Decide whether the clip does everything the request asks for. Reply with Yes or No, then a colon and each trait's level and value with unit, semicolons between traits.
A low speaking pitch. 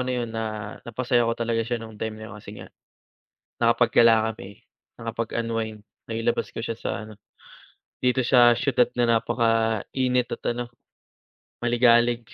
Yes: low, 115 Hz